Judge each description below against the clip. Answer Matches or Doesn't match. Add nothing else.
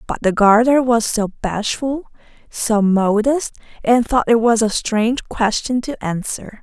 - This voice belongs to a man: Doesn't match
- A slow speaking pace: Doesn't match